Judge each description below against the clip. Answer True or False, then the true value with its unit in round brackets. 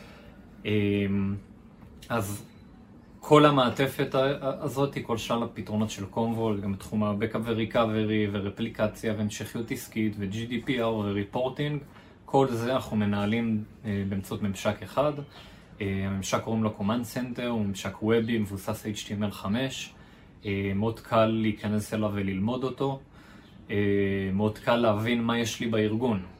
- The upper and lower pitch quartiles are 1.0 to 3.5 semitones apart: True (2.4 semitones)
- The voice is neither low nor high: False (110 Hz)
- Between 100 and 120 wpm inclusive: True (110 wpm)